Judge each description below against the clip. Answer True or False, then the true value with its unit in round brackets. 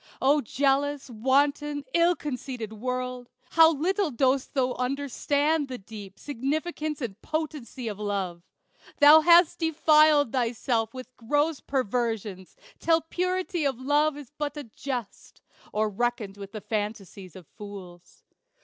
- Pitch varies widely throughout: False (5.0 semitones)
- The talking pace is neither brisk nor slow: False (130 wpm)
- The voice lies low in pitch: False (265 Hz)